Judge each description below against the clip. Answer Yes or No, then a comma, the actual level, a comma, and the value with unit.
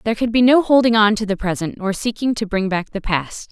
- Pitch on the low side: No, high, 210 Hz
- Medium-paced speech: No, fast, 275 wpm